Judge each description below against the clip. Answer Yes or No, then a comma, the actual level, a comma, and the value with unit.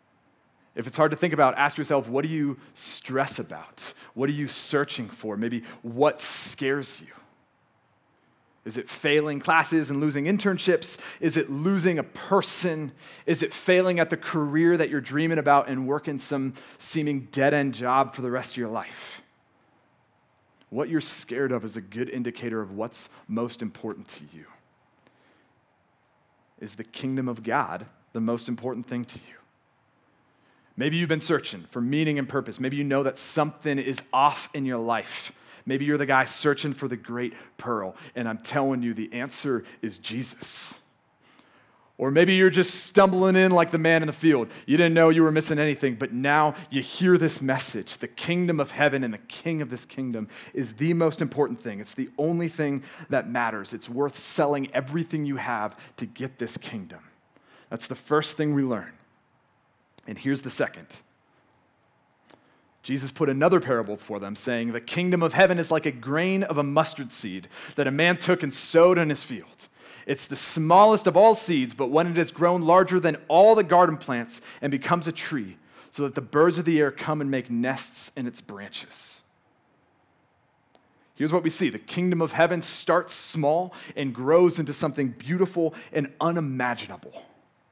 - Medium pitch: Yes, medium, 145 Hz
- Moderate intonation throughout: Yes, average, 4.3 semitones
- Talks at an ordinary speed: Yes, average, 180 wpm